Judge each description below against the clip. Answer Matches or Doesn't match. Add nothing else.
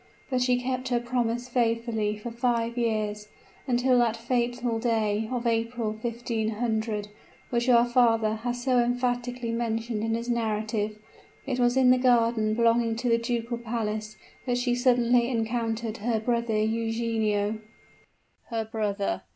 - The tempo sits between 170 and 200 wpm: Doesn't match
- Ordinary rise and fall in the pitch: Doesn't match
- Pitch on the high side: Matches